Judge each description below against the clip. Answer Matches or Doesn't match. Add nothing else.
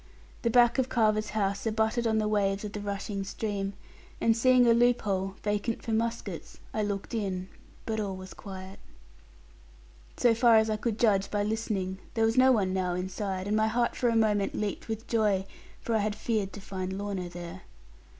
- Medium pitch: Doesn't match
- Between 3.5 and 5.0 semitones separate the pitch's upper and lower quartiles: Doesn't match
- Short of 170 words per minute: Doesn't match